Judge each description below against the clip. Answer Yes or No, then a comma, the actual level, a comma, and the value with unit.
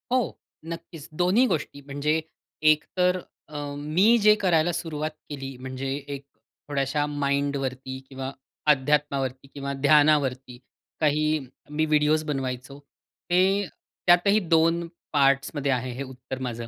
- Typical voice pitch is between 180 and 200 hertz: No, medium, 145 Hz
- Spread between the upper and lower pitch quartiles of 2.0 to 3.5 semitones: Yes, average, 2.9 semitones